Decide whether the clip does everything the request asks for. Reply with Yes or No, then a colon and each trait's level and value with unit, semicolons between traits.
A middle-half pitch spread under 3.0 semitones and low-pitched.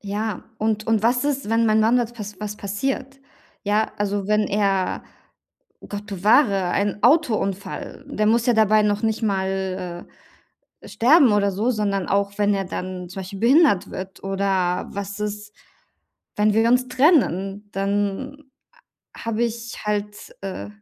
No: narrow, 2.5 semitones; high, 210 Hz